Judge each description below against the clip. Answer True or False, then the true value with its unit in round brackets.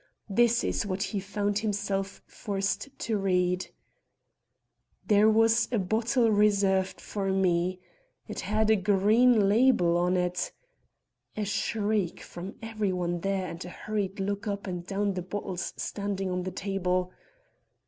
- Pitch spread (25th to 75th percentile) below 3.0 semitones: True (2.5 semitones)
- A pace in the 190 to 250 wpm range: False (150 wpm)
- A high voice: True (200 Hz)